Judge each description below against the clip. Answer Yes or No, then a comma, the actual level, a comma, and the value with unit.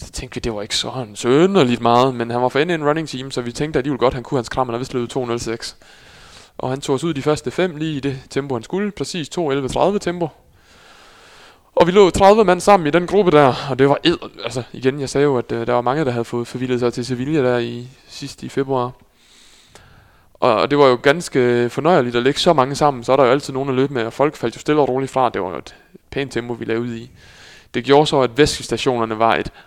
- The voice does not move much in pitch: No, average, 3.4 semitones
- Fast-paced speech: Yes, fast, 265 wpm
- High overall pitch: No, low, 130 Hz